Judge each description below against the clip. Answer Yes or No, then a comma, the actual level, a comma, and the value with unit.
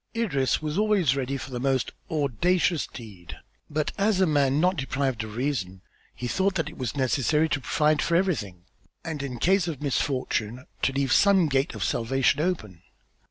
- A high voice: No, medium, 140 Hz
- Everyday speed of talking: Yes, average, 175 wpm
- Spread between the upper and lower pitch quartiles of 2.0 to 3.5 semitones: No, average, 4.6 semitones